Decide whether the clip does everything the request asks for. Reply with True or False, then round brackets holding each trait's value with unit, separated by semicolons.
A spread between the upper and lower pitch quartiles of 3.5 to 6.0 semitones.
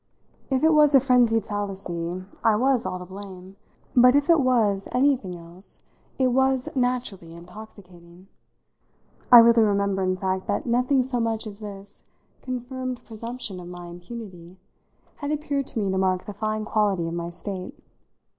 True (5.2 semitones)